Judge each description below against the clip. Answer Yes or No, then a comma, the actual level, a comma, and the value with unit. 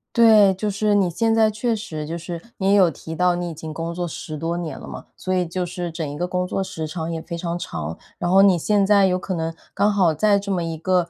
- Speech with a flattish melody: No, average, 3.2 semitones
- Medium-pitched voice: Yes, medium, 180 Hz